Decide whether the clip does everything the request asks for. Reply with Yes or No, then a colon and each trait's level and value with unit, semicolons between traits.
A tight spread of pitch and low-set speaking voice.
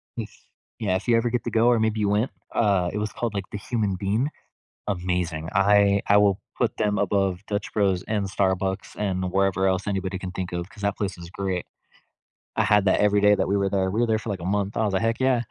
Yes: narrow, 1.9 semitones; low, 100 Hz